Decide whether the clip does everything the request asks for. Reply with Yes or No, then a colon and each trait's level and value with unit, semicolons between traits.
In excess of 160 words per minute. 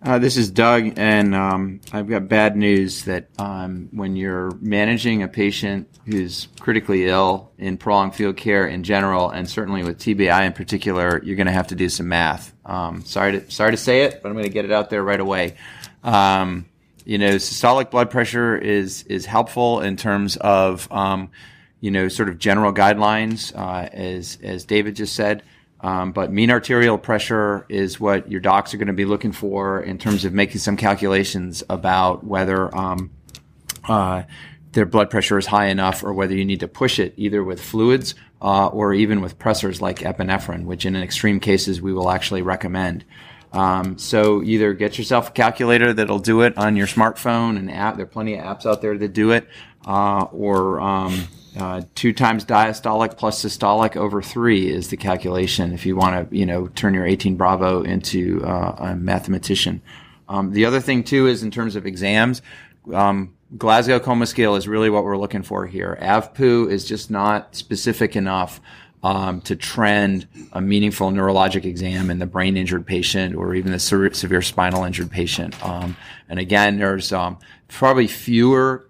Yes: average, 185 wpm